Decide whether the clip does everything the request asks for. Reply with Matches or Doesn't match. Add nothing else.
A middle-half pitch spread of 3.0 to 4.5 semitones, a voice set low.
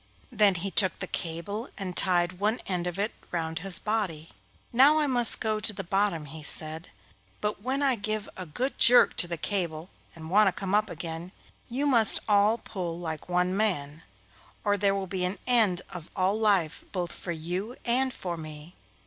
Doesn't match